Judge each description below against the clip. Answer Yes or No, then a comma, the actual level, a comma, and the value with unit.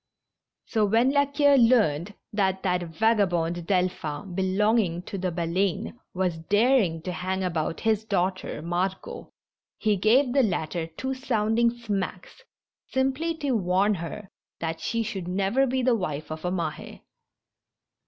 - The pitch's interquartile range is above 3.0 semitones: Yes, average, 4.8 semitones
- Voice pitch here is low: No, high, 195 Hz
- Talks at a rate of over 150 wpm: No, average, 145 wpm